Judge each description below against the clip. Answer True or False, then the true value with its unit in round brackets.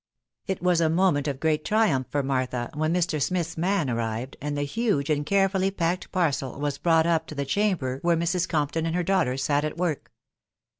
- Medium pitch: True (160 Hz)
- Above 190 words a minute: True (200 wpm)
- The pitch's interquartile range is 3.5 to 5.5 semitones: True (4.2 semitones)